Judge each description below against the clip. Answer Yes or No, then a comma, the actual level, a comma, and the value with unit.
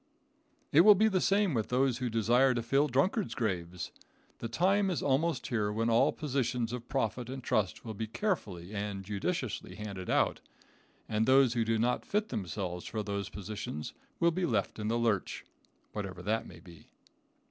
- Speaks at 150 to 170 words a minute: No, average, 180 wpm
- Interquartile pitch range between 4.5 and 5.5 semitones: Yes, average, 4.8 semitones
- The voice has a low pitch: Yes, low, 115 Hz